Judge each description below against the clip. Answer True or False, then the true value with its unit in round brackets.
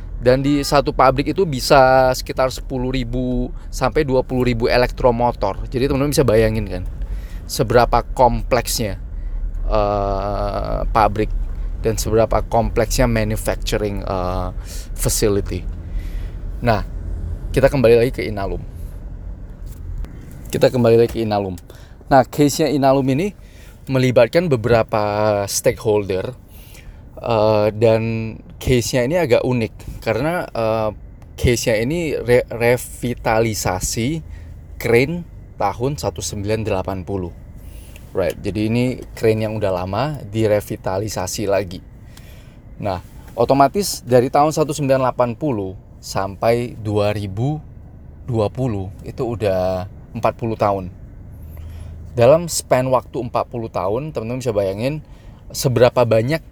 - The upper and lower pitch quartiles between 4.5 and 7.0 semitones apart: True (4.9 semitones)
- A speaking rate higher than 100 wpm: False (95 wpm)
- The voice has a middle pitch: False (110 Hz)